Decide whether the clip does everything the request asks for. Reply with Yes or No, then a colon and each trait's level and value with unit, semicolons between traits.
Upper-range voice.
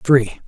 No: low, 125 Hz